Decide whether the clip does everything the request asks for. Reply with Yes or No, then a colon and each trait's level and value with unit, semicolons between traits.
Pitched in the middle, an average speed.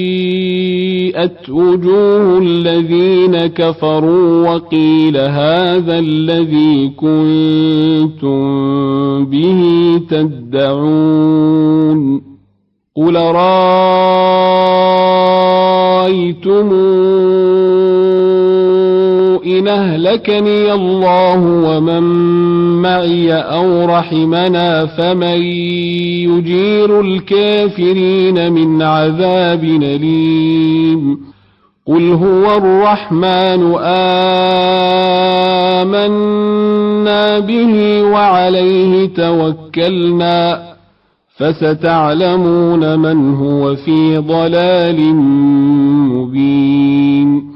No: medium, 175 Hz; slow, 45 wpm